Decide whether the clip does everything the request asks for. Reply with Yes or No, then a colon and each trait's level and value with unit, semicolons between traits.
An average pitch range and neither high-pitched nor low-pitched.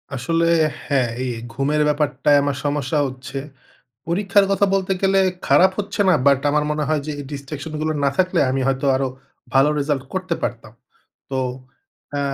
Yes: average, 3.7 semitones; medium, 150 Hz